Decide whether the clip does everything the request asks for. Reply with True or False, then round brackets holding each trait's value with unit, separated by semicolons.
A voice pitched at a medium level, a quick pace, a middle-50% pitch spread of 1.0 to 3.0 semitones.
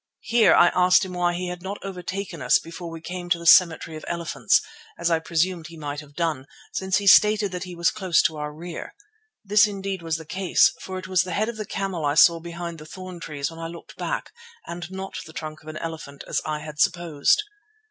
True (175 Hz; 230 wpm; 2.6 semitones)